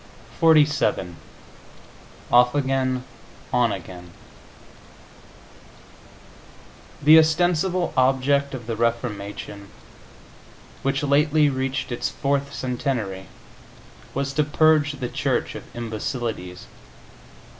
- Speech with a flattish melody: No, average, 3.8 semitones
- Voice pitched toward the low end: Yes, low, 130 Hz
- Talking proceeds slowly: Yes, slow, 80 wpm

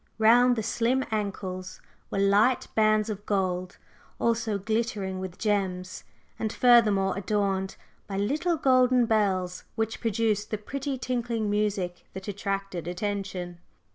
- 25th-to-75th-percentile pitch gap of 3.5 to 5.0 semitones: No, average, 3.0 semitones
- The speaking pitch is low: No, high, 205 Hz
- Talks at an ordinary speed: No, slow, 125 wpm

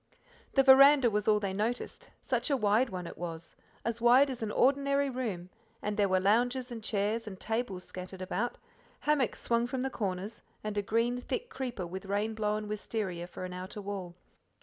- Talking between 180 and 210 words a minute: Yes, average, 190 wpm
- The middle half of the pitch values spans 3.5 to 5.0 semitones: Yes, average, 4.3 semitones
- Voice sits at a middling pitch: No, high, 215 Hz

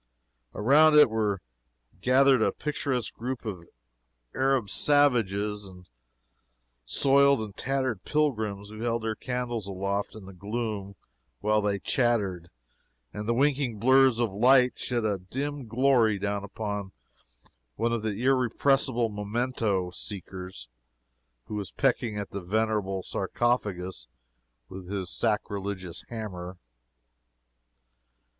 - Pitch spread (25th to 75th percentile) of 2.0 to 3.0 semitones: No, average, 4.1 semitones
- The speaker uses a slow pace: Yes, slow, 115 wpm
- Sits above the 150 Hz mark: No, low, 110 Hz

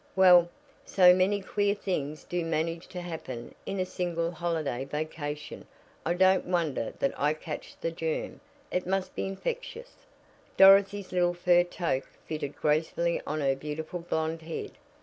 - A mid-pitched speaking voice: Yes, medium, 170 Hz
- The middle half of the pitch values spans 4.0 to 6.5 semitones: No, average, 3.0 semitones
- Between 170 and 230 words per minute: No, average, 150 wpm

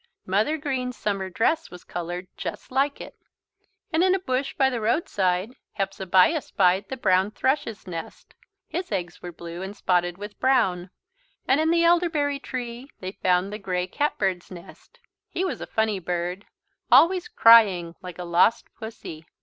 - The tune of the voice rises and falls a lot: Yes, wide, 7.1 semitones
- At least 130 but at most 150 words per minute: No, average, 165 wpm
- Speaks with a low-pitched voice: No, high, 205 Hz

